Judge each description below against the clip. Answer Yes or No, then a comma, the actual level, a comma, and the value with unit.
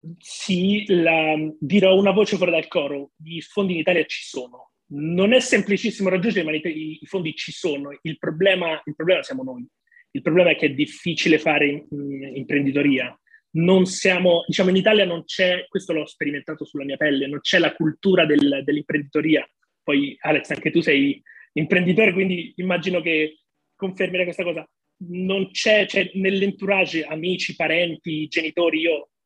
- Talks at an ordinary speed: Yes, average, 160 wpm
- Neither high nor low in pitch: Yes, medium, 170 Hz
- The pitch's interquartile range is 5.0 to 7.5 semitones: No, average, 3.6 semitones